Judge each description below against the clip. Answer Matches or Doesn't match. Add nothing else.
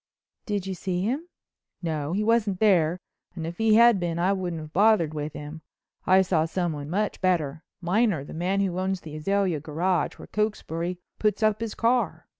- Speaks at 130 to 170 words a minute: Doesn't match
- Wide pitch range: Doesn't match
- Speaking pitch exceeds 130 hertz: Matches